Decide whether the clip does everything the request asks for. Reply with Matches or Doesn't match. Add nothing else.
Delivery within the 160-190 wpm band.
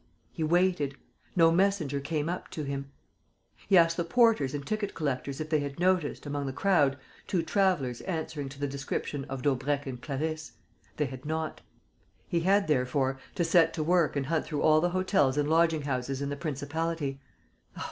Matches